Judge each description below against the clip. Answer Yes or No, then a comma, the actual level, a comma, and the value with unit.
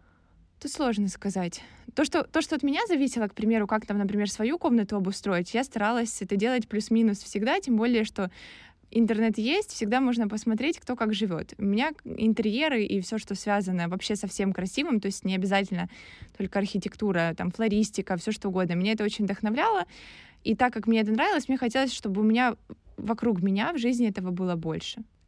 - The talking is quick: Yes, fast, 190 wpm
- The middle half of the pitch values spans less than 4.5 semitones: Yes, average, 3.2 semitones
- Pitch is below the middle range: No, high, 215 Hz